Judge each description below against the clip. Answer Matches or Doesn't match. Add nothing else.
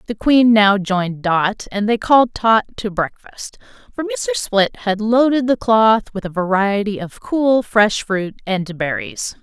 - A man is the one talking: Doesn't match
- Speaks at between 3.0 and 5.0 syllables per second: Matches